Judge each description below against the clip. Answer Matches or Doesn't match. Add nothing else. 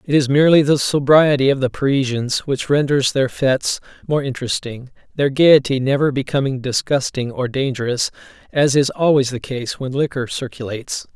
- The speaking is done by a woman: Doesn't match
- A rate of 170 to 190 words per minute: Doesn't match